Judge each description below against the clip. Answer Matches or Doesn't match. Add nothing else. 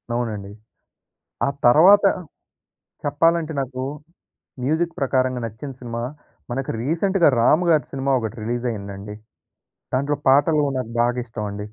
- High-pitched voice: Doesn't match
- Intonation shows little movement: Doesn't match